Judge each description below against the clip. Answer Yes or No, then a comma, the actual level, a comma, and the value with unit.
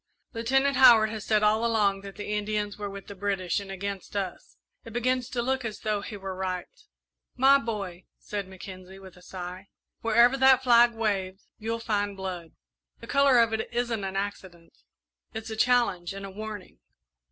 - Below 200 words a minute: Yes, average, 180 wpm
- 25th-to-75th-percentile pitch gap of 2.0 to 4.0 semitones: Yes, average, 3.2 semitones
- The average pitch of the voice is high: Yes, high, 210 Hz